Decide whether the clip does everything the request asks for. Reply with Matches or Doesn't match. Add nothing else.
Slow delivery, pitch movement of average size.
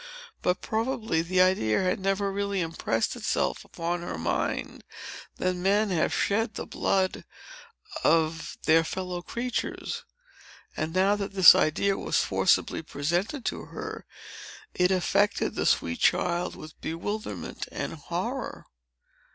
Matches